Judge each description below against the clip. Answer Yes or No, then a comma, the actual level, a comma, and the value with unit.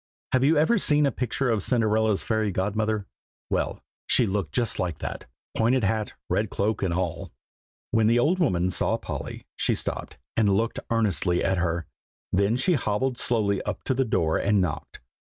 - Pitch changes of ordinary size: Yes, average, 4.1 semitones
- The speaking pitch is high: No, low, 110 Hz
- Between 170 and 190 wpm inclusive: Yes, average, 175 wpm